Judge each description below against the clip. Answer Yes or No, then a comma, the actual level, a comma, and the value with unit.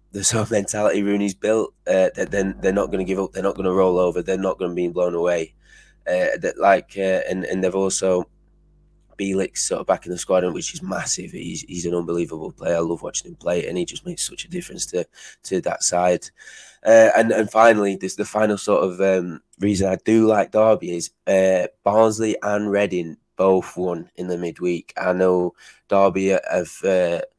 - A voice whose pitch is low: Yes, very low, 95 Hz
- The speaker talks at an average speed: No, fast, 210 wpm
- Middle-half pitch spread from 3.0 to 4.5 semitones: No, narrow, 2.6 semitones